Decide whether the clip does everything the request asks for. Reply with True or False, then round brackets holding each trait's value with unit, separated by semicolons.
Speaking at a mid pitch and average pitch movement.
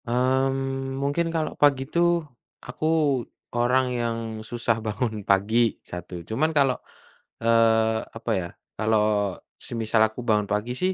False (120 Hz; 3.3 semitones)